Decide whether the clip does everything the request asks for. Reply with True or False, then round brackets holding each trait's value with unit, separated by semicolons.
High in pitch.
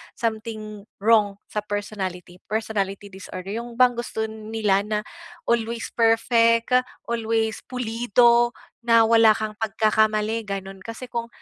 True (220 Hz)